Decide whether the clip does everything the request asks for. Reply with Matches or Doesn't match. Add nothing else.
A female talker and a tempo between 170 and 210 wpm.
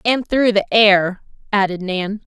Doesn't match